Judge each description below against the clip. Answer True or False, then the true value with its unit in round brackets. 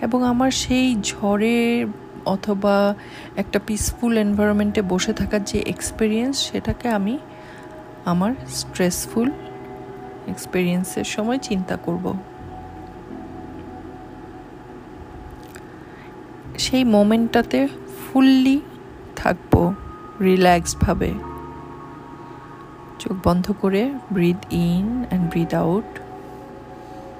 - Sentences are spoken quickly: False (75 wpm)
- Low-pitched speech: False (210 Hz)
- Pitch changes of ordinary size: True (3.9 semitones)